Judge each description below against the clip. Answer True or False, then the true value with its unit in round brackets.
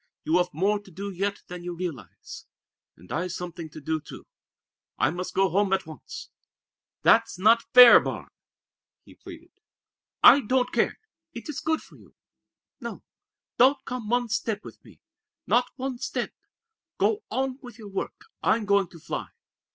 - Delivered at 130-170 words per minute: True (165 wpm)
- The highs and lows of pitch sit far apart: True (5.8 semitones)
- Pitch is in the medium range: False (205 Hz)